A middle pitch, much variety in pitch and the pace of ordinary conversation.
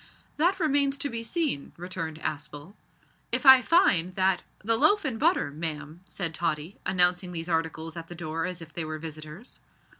Yes: medium, 175 Hz; wide, 7.3 semitones; average, 180 wpm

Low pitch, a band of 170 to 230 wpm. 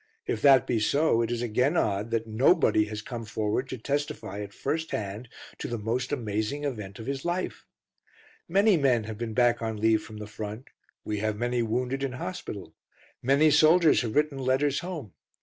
Yes: low, 120 Hz; average, 185 wpm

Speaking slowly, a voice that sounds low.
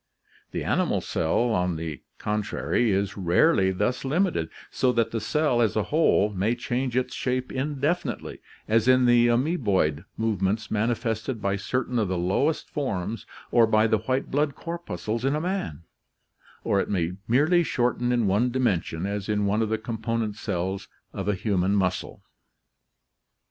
No: average, 160 wpm; low, 110 Hz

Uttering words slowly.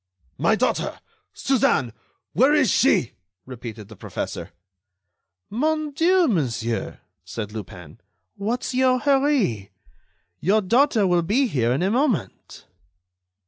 Yes: slow, 110 wpm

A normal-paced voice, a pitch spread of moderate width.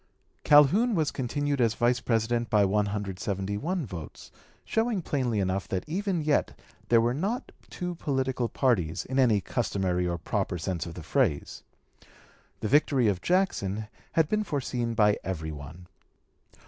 No: average, 145 wpm; wide, 7.1 semitones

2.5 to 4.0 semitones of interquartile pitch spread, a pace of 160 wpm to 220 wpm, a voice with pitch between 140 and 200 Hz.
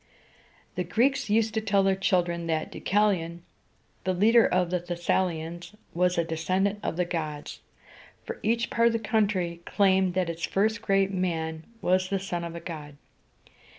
Yes: average, 3.2 semitones; average, 185 wpm; medium, 185 Hz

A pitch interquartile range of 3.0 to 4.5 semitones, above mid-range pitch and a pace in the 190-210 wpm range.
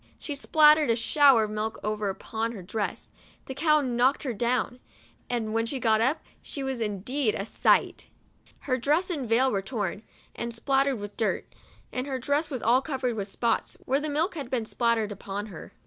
Yes: average, 4.1 semitones; high, 240 Hz; average, 195 wpm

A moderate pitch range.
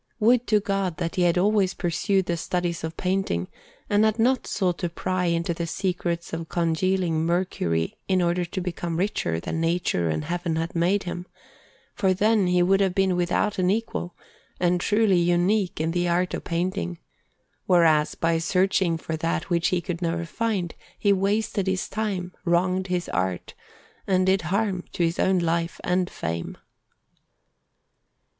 No: narrow, 2.3 semitones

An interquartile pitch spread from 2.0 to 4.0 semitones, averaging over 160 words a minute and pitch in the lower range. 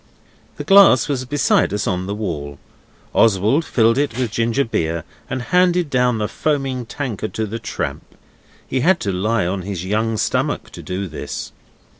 No: average, 5.1 semitones; average, 170 wpm; low, 115 Hz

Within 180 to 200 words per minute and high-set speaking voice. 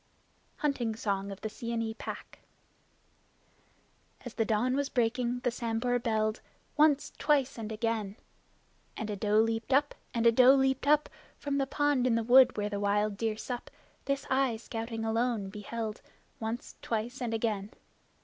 No: average, 160 wpm; high, 230 Hz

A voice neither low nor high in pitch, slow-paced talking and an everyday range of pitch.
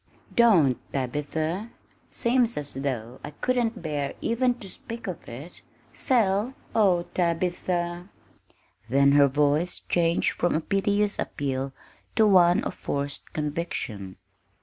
No: medium, 170 Hz; slow, 120 wpm; wide, 6.4 semitones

